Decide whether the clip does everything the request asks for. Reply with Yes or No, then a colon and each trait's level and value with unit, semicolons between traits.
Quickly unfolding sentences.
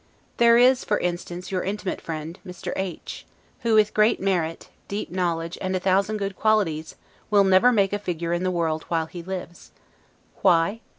No: average, 175 wpm